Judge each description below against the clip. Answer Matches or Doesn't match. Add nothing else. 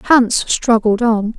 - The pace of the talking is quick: Doesn't match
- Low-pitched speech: Doesn't match